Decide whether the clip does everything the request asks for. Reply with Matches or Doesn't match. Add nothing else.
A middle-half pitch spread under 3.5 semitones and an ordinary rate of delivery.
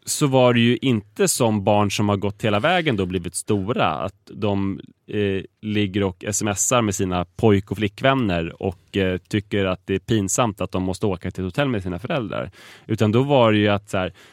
Doesn't match